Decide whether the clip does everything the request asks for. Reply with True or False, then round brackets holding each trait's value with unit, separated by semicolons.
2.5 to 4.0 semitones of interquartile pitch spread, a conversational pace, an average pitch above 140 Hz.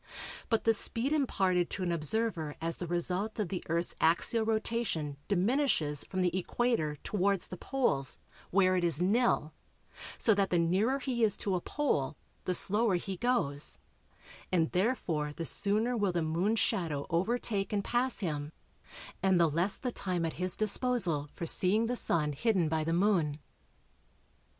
False (5.0 semitones; 165 wpm; 185 Hz)